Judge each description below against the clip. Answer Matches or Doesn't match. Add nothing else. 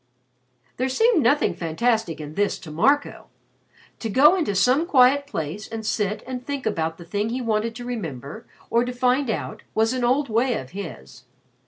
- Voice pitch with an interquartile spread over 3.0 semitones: Matches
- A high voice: Matches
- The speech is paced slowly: Doesn't match